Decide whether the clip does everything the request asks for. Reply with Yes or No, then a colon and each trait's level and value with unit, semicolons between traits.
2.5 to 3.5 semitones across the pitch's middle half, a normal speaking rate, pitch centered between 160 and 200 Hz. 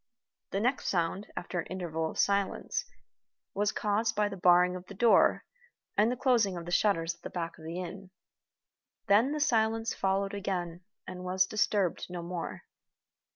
Yes: average, 2.9 semitones; average, 170 wpm; high, 190 Hz